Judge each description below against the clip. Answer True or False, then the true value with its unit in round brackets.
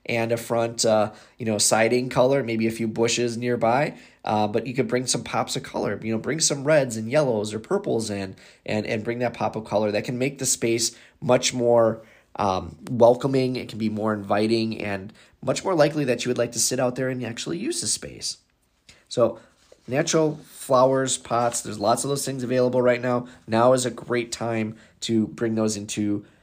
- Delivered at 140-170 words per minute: False (205 wpm)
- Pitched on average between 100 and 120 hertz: True (115 Hz)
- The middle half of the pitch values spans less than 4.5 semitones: True (2.4 semitones)